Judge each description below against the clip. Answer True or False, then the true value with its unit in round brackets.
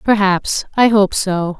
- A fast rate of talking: False (150 wpm)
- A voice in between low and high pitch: False (200 Hz)